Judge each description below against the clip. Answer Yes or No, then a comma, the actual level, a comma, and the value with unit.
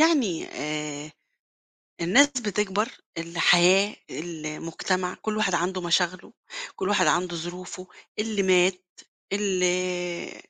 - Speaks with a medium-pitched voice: Yes, medium, 180 Hz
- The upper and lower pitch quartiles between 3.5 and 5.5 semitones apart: No, narrow, 2.5 semitones